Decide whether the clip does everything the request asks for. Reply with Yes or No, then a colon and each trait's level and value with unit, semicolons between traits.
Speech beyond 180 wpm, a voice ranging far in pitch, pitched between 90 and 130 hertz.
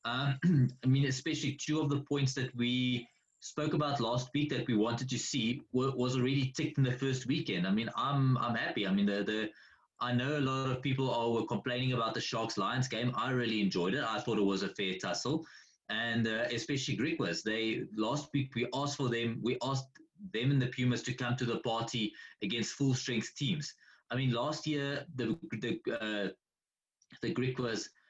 No: fast, 205 wpm; average, 3.3 semitones; low, 125 Hz